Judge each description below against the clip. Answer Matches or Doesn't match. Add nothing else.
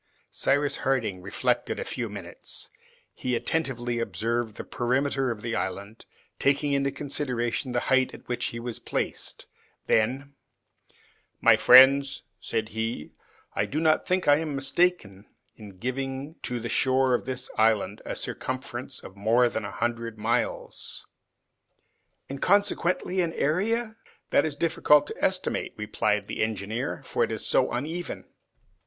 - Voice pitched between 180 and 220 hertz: Doesn't match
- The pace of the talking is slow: Doesn't match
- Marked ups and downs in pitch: Doesn't match